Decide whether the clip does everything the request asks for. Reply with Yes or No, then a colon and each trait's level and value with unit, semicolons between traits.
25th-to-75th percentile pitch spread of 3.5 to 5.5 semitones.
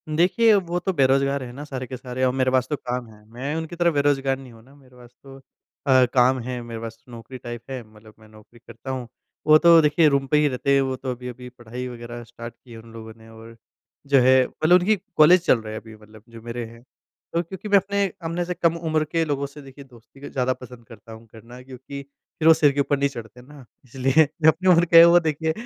Yes: average, 4.2 semitones